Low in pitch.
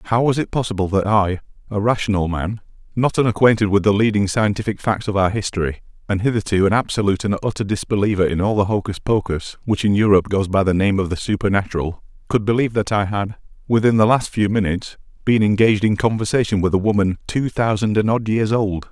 Yes: low, 105 Hz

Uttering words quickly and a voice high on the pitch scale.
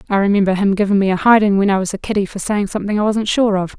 Yes: fast, 300 wpm; high, 200 Hz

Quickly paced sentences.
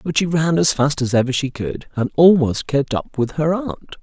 Yes: fast, 240 wpm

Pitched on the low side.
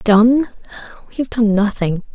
No: high, 220 Hz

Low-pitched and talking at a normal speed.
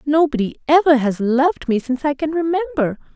No: very high, 290 Hz; average, 170 wpm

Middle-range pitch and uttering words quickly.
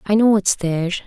No: high, 195 Hz; fast, 225 wpm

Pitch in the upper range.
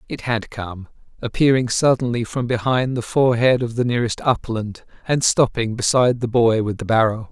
No: low, 120 Hz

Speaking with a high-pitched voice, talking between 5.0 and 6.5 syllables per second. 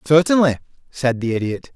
No: medium, 140 Hz; 5.3 syllables/s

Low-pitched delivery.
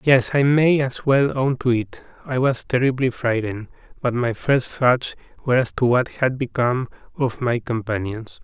Yes: low, 125 Hz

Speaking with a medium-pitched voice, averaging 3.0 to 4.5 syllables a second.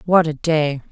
Yes: medium, 155 Hz; 4.2 syllables/s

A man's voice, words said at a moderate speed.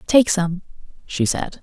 No: female; average, 150 wpm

